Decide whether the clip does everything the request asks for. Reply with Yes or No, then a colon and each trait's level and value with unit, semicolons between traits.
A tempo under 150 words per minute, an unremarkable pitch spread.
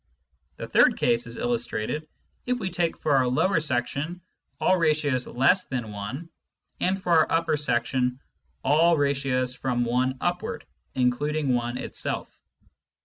Yes: average, 140 wpm; average, 4.9 semitones